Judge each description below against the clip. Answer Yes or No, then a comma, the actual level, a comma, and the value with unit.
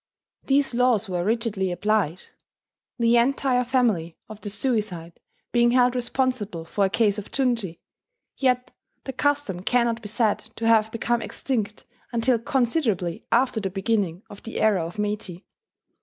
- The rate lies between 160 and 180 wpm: No, average, 145 wpm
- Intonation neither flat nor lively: Yes, average, 3.9 semitones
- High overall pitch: Yes, high, 225 Hz